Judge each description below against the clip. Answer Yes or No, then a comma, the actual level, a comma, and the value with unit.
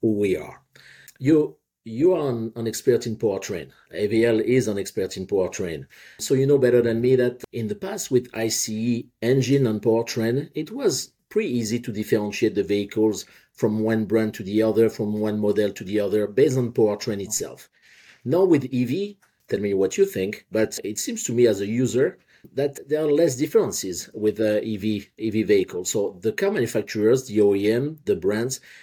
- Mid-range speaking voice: No, low, 115 Hz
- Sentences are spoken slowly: No, average, 185 wpm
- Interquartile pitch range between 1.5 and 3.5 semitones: No, average, 3.9 semitones